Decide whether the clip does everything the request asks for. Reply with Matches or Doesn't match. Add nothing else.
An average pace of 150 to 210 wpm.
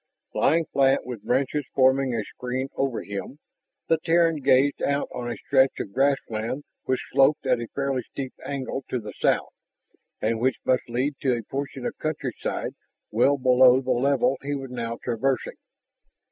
Matches